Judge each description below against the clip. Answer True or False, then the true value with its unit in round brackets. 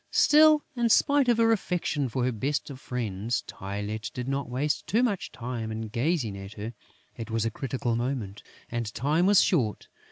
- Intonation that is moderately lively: False (7.3 semitones)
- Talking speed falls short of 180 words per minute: False (185 wpm)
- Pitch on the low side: True (125 Hz)